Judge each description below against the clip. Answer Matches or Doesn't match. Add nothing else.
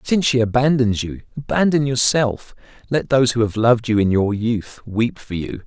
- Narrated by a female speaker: Doesn't match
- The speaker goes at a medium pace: Matches